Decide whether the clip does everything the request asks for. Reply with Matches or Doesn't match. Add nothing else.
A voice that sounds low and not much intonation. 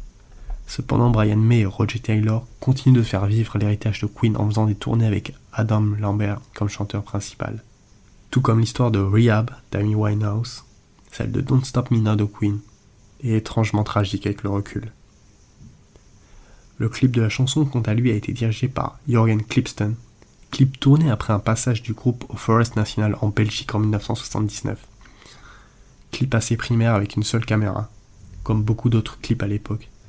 Matches